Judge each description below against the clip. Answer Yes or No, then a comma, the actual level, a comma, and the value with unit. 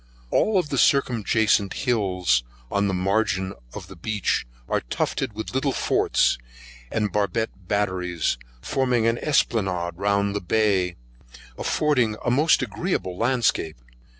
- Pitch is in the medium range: No, low, 105 Hz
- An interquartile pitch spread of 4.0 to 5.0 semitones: Yes, average, 4.4 semitones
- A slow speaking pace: Yes, slow, 125 wpm